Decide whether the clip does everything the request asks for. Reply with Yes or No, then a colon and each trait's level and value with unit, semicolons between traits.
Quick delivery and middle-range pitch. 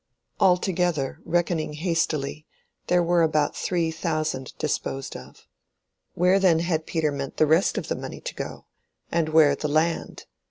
No: average, 145 wpm; medium, 160 Hz